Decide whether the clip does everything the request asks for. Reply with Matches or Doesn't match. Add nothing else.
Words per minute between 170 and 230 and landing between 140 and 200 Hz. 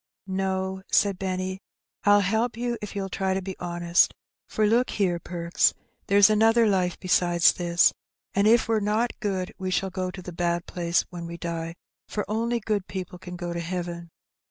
Matches